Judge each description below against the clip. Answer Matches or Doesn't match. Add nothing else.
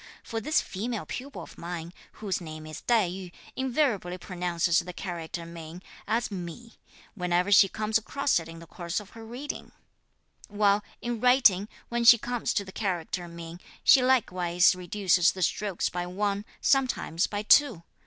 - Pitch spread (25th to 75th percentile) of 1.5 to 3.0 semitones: Doesn't match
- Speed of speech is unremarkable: Matches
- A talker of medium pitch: Doesn't match